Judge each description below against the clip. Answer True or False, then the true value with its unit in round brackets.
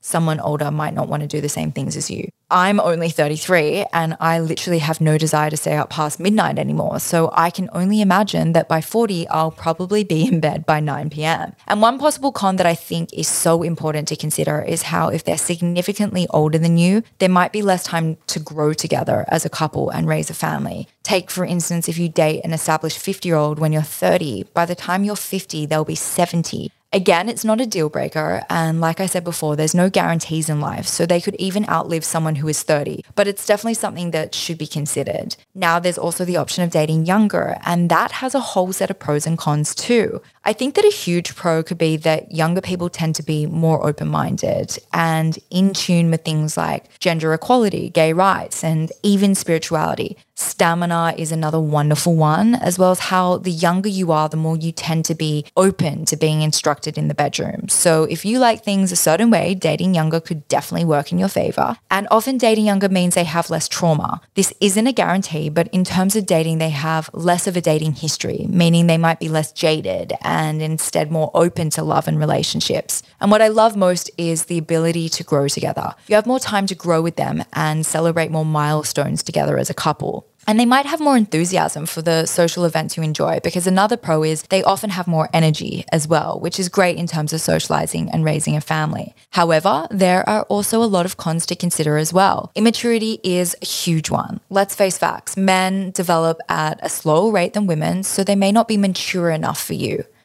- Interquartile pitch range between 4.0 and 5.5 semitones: False (3.3 semitones)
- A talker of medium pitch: True (170 Hz)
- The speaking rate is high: True (215 wpm)